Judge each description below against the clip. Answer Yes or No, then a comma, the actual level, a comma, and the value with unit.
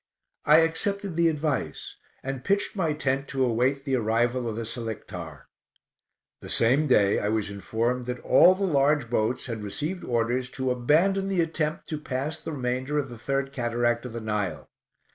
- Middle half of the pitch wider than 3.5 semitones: Yes, average, 4.7 semitones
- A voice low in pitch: Yes, low, 130 Hz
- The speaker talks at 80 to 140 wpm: No, average, 175 wpm